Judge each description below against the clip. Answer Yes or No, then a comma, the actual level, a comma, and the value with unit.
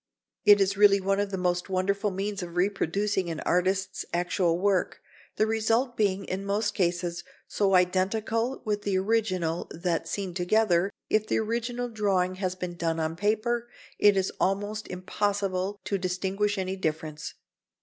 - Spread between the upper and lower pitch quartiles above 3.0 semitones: No, narrow, 2.4 semitones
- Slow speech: No, average, 155 wpm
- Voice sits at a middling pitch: No, high, 195 Hz